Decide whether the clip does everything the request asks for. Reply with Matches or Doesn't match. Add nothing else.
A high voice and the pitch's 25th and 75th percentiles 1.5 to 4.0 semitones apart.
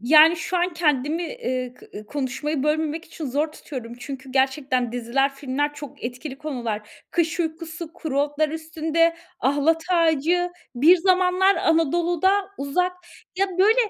Matches